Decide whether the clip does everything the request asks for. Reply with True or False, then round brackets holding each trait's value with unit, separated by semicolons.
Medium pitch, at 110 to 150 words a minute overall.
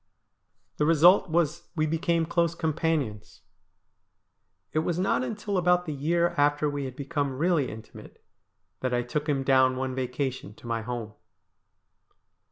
True (150 Hz; 145 wpm)